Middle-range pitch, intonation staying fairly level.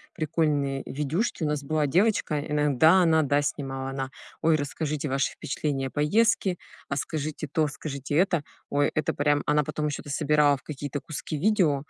Yes: medium, 150 Hz; narrow, 1.9 semitones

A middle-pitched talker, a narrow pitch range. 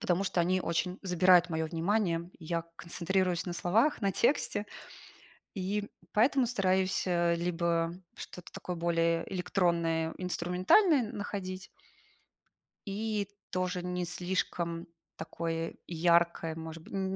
Yes: medium, 180 Hz; narrow, 2.2 semitones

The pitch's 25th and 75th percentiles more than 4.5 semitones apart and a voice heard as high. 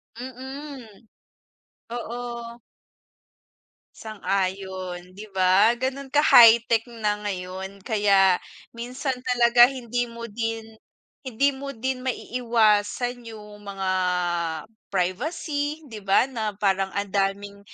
No: average, 3.9 semitones; high, 230 Hz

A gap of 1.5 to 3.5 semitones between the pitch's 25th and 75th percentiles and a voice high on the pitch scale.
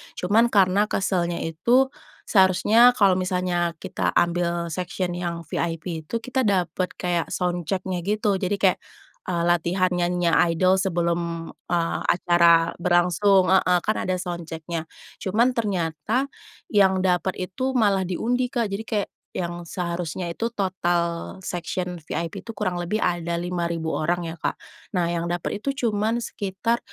No: average, 2.7 semitones; medium, 180 Hz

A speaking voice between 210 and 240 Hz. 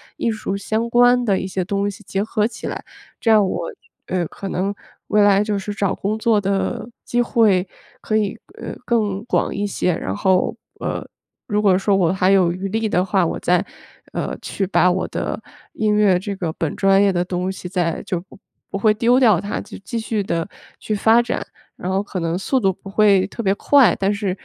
No: high, 200 Hz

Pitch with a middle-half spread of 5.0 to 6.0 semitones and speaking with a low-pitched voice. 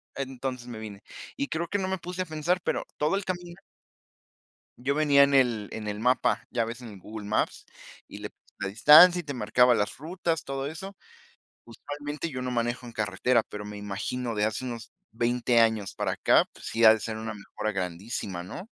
Yes: wide, 5.4 semitones; low, 125 Hz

